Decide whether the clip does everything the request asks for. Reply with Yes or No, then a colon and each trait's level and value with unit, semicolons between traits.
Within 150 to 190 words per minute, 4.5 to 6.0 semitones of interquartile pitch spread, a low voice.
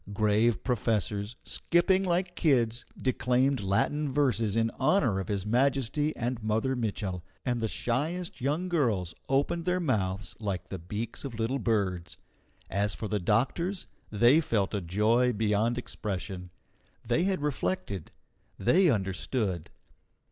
No: slow, 135 wpm; average, 5.3 semitones; low, 115 Hz